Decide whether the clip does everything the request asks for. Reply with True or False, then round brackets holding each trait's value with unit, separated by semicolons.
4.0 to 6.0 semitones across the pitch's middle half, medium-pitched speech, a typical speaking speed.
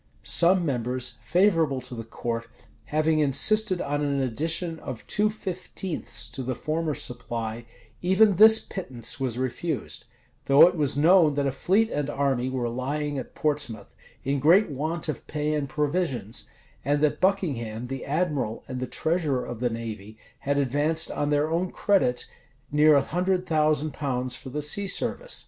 True (4.7 semitones; 145 Hz; 165 wpm)